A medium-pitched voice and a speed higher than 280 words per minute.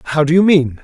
Yes: medium, 155 Hz; fast, 290 wpm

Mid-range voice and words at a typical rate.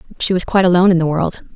No: medium, 175 Hz; fast, 270 wpm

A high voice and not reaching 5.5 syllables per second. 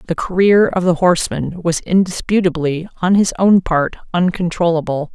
No: medium, 175 Hz; 5.0 syllables/s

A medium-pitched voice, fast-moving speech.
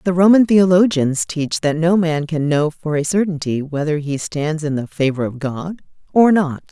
No: medium, 160 Hz; average, 195 wpm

